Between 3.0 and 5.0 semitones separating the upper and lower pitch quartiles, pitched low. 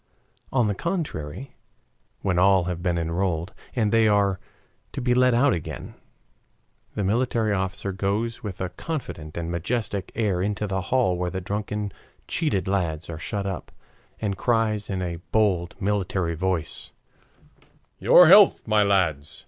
Yes: average, 3.6 semitones; low, 100 Hz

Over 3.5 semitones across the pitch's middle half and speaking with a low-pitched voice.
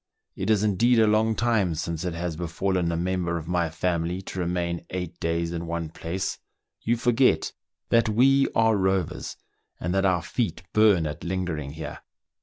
Yes: average, 4.2 semitones; very low, 90 Hz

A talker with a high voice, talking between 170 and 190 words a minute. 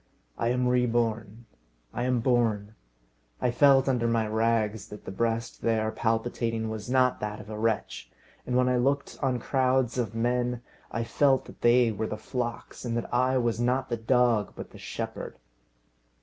No: low, 120 Hz; average, 175 wpm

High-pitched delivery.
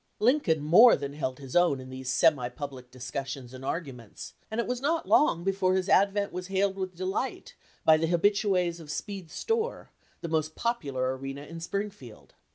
No: medium, 170 Hz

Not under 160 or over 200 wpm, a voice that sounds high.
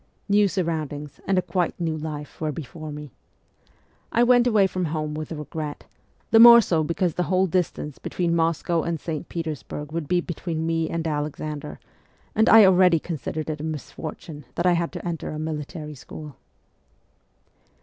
No: average, 170 wpm; medium, 160 Hz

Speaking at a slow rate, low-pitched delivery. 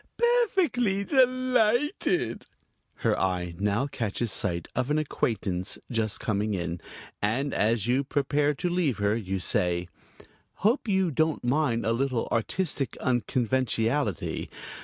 Yes: slow, 120 wpm; low, 125 Hz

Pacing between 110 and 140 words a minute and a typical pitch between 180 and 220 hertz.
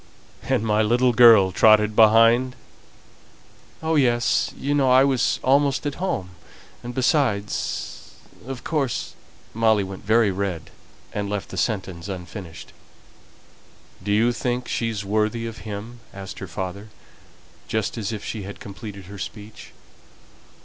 No: slow, 135 wpm; low, 110 Hz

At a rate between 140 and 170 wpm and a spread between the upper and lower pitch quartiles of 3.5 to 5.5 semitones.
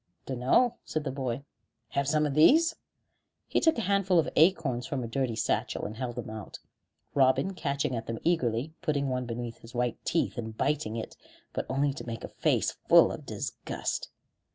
No: average, 185 wpm; average, 4.7 semitones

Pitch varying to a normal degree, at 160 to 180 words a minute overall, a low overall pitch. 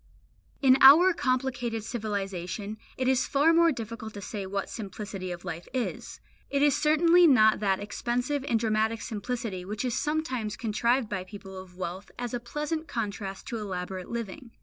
No: average, 4.6 semitones; average, 165 wpm; high, 225 Hz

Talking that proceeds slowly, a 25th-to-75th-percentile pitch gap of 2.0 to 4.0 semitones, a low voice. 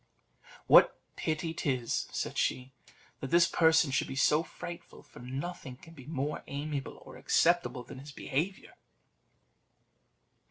No: slow, 130 wpm; average, 3.6 semitones; medium, 150 Hz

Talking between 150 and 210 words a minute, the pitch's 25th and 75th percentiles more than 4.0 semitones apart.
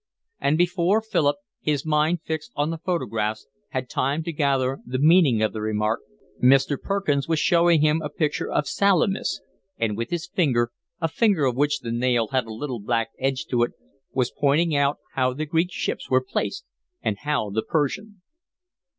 Yes: average, 180 wpm; average, 4.7 semitones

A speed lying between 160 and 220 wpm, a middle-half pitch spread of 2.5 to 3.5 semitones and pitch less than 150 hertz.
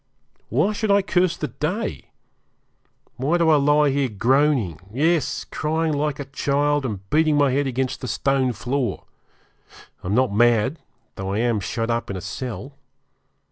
No: average, 165 wpm; average, 4.2 semitones; low, 135 Hz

